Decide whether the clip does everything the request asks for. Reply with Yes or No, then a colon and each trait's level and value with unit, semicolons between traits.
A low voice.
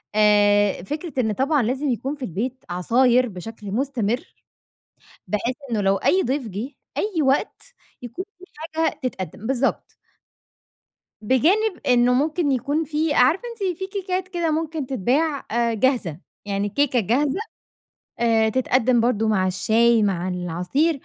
No: very high, 250 Hz